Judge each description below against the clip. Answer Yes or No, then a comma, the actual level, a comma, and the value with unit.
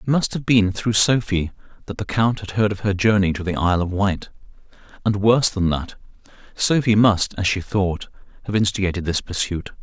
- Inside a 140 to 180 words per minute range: No, average, 195 wpm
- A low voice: Yes, low, 100 Hz